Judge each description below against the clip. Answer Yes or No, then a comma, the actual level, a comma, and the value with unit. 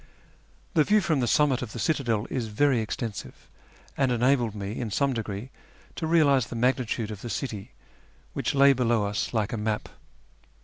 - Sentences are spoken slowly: No, average, 175 wpm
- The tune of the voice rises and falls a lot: No, average, 4.1 semitones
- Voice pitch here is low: Yes, low, 120 Hz